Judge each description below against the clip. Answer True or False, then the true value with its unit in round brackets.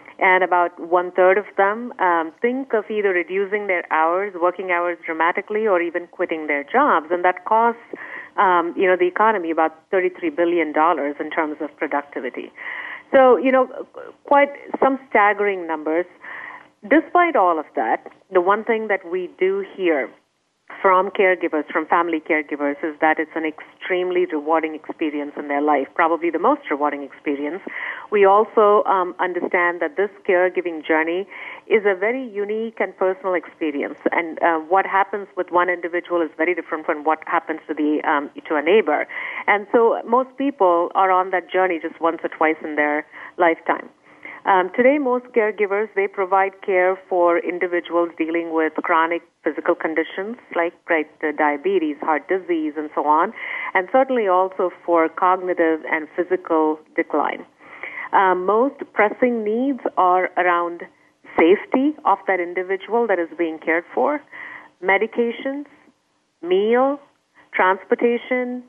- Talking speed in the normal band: True (150 wpm)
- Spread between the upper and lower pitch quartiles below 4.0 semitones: False (4.9 semitones)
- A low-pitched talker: False (185 Hz)